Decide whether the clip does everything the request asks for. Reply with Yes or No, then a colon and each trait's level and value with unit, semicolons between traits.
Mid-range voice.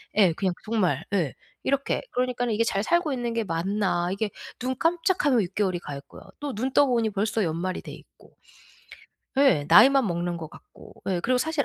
No: high, 215 Hz